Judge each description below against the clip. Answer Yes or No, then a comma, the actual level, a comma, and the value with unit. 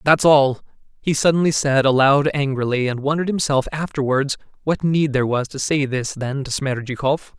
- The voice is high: No, medium, 140 Hz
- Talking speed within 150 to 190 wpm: Yes, average, 170 wpm